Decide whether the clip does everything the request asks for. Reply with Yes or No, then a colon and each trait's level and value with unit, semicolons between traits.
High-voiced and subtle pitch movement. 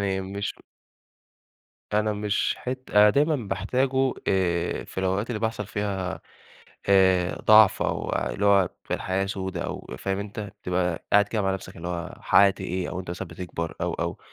No: very low, 95 Hz; narrow, 2.1 semitones